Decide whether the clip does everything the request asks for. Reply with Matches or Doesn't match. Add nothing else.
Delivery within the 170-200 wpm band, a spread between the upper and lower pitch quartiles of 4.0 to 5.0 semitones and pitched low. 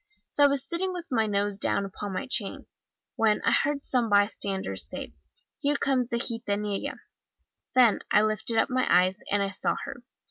Doesn't match